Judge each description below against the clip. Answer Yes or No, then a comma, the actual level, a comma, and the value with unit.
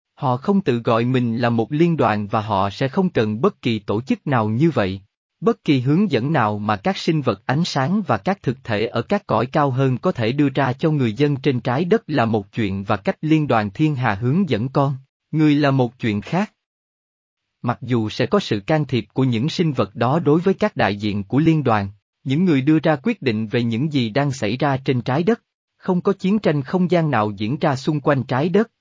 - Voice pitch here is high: No, medium, 140 Hz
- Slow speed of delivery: No, average, 240 wpm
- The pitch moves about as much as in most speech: No, wide, 5.9 semitones